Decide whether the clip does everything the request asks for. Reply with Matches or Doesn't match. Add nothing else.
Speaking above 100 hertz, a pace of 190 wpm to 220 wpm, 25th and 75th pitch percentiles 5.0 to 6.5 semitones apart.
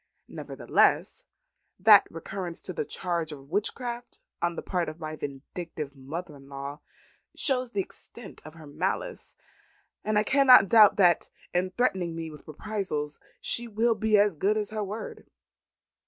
Doesn't match